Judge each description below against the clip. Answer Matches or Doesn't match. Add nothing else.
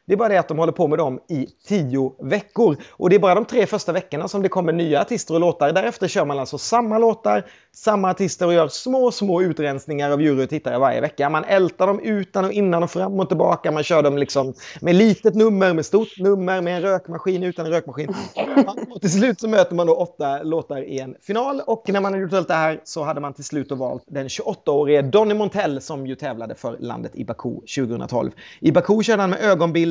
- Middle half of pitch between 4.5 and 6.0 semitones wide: Matches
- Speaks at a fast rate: Matches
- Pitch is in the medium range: Matches